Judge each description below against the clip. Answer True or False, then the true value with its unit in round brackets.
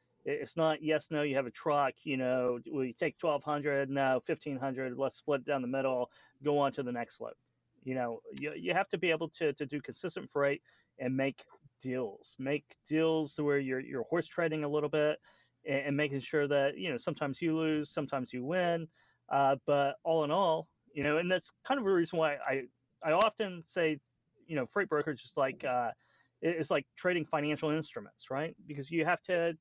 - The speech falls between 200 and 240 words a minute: True (205 wpm)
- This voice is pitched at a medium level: True (150 Hz)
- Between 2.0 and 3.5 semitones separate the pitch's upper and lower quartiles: True (2.9 semitones)